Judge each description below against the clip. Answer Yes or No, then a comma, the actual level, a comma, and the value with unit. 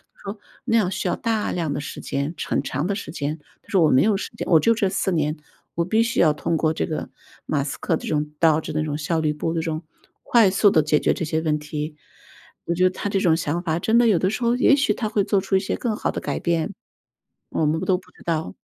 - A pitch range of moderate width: Yes, average, 4.4 semitones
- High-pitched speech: No, medium, 170 Hz